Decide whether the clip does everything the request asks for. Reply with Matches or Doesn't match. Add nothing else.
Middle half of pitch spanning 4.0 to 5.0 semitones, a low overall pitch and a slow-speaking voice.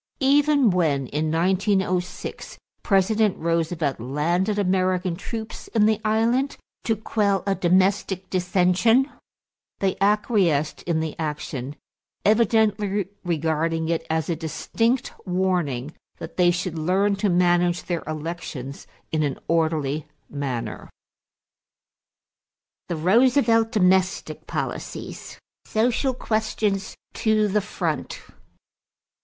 Doesn't match